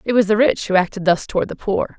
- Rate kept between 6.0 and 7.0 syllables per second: Yes, 6.4 syllables/s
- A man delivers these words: No, female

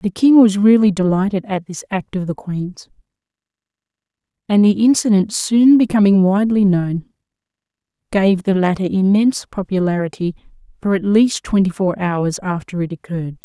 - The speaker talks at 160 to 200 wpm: No, average, 145 wpm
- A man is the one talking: No, female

